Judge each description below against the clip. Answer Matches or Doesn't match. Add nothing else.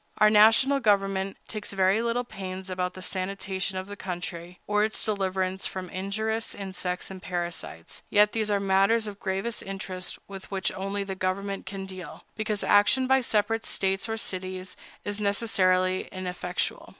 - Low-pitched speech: Doesn't match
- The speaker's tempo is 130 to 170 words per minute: Matches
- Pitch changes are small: Matches